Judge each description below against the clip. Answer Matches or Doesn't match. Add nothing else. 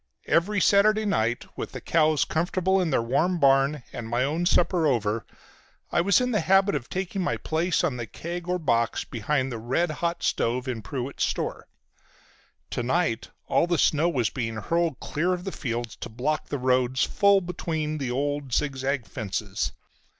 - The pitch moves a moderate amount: Doesn't match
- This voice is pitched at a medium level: Matches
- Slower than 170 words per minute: Doesn't match